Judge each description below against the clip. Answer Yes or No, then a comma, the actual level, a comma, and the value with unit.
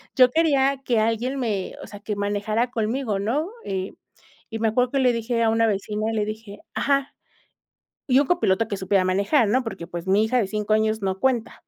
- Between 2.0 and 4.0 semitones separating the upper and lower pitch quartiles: Yes, average, 3.7 semitones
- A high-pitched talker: Yes, high, 220 Hz